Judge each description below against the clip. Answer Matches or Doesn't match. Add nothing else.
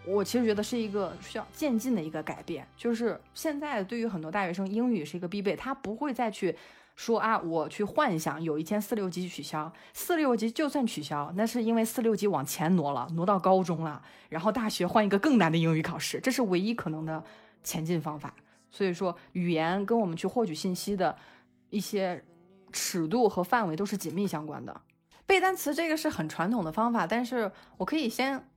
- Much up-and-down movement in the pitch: Matches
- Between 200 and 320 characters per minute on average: Matches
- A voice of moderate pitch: Doesn't match